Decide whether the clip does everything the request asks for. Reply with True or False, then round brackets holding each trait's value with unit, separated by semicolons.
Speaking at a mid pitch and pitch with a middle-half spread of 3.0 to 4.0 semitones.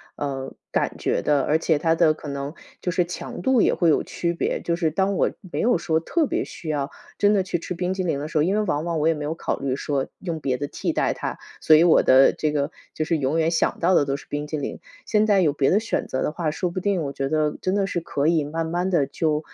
True (160 Hz; 3.4 semitones)